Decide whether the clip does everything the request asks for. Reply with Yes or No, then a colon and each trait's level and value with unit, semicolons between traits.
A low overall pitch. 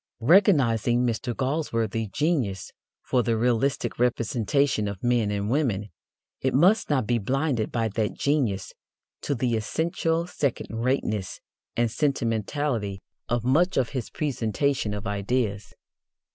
Yes: low, 120 Hz